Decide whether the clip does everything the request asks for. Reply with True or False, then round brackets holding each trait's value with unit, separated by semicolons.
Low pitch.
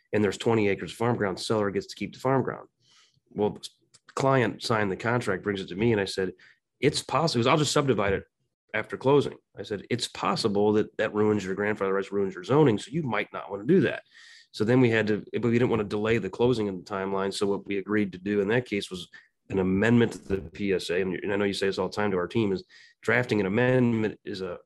True (105 Hz)